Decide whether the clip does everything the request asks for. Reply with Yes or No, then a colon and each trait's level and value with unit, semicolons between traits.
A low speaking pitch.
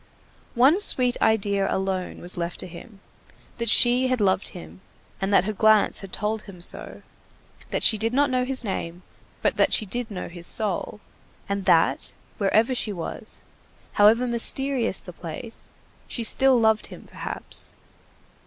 No: high, 215 Hz